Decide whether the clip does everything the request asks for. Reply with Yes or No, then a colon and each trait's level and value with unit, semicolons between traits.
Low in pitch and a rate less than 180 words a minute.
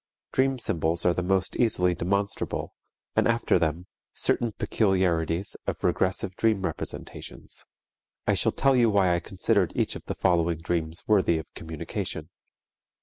Yes: very low, 90 Hz; average, 145 wpm